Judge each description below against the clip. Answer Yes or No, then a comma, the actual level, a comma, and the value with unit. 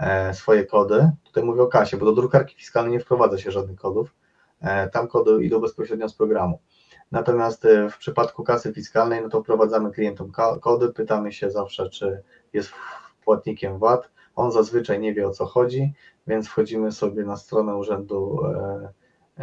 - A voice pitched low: Yes, low, 110 Hz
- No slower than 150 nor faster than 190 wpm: Yes, average, 155 wpm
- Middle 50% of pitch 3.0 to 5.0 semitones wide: No, narrow, 2.6 semitones